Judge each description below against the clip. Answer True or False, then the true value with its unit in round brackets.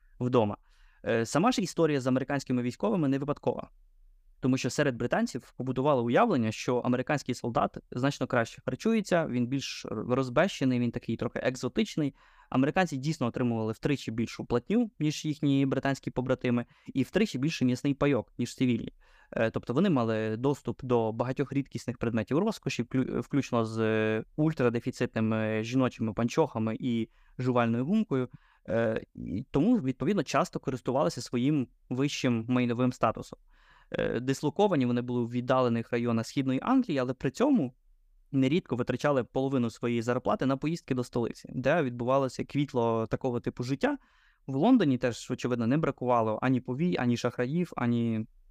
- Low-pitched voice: True (130 Hz)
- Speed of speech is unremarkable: True (135 wpm)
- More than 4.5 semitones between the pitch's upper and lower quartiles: False (3.0 semitones)